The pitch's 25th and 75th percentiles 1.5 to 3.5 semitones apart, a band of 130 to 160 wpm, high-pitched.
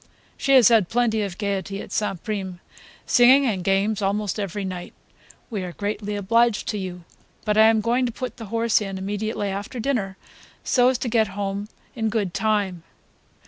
No: average, 2.7 semitones; average, 185 wpm; high, 210 Hz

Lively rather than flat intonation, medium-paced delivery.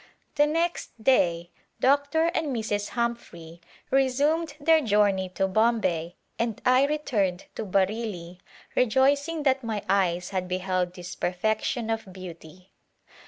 No: wide, 6.5 semitones; slow, 125 wpm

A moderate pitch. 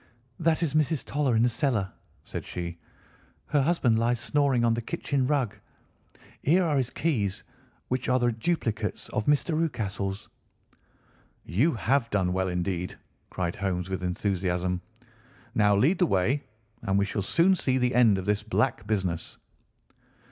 No: low, 115 Hz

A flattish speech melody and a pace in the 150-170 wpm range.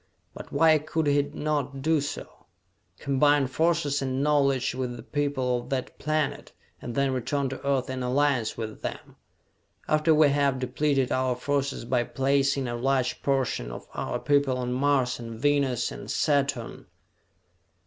Yes: narrow, 2.2 semitones; average, 155 wpm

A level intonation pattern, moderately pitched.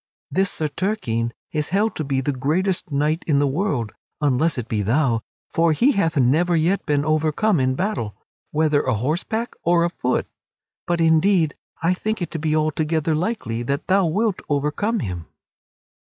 No: average, 4.5 semitones; medium, 155 Hz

